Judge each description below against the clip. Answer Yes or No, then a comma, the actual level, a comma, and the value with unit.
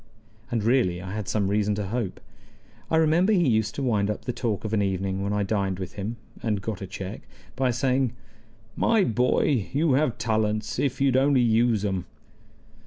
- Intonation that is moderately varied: Yes, average, 4.1 semitones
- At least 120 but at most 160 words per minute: No, average, 190 wpm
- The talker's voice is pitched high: No, low, 110 Hz